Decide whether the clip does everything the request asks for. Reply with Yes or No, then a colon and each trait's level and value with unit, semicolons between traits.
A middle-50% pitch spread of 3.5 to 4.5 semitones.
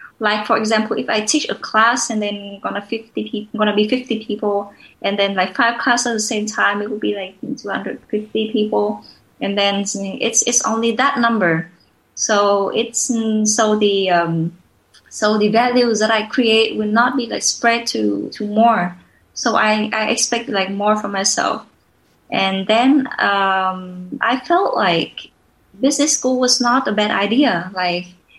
No: average, 2.8 semitones